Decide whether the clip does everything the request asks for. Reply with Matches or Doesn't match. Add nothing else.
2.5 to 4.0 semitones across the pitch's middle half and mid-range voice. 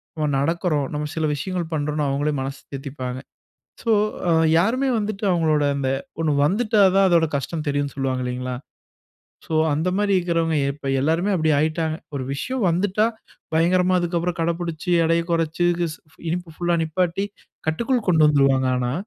Matches